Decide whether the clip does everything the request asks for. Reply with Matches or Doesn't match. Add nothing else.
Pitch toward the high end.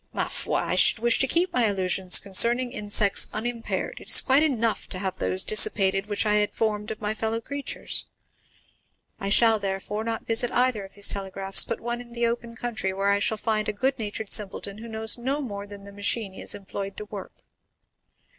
Matches